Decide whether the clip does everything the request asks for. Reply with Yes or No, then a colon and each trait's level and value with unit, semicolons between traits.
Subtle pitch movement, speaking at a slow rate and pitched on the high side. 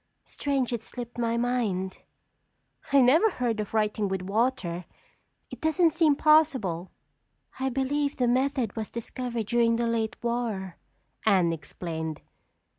No: average, 4.7 semitones; slow, 130 wpm; high, 235 Hz